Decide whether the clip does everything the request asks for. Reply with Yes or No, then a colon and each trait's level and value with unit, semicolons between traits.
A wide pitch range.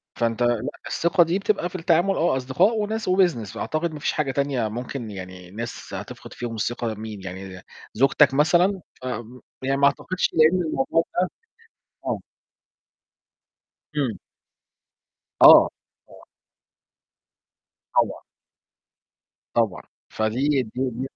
Yes: wide, 6.9 semitones